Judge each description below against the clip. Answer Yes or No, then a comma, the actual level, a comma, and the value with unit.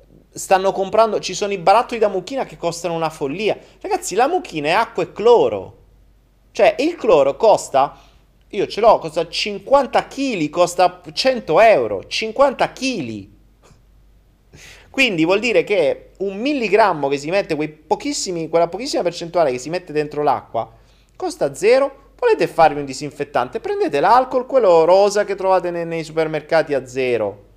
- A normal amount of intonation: No, wide, 8.7 semitones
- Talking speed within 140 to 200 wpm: Yes, average, 150 wpm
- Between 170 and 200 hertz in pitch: Yes, high, 190 Hz